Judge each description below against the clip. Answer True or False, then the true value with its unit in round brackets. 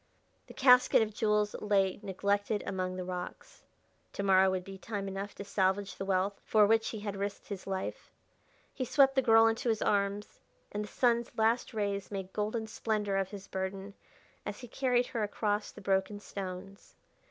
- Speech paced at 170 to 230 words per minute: True (180 wpm)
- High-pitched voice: True (205 Hz)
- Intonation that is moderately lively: False (2.2 semitones)